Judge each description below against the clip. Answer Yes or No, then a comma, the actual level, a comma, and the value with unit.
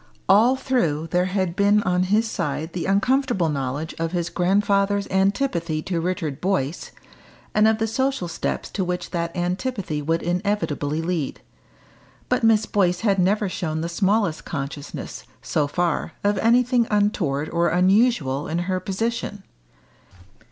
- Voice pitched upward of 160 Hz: Yes, medium, 185 Hz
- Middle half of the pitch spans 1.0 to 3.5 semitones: No, average, 4.0 semitones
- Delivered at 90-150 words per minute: Yes, average, 145 wpm